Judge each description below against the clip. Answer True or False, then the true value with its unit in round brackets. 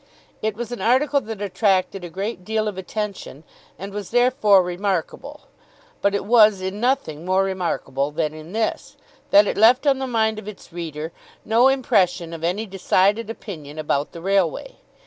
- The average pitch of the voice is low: False (200 Hz)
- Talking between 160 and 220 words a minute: True (170 wpm)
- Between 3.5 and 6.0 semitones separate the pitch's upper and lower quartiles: True (4.0 semitones)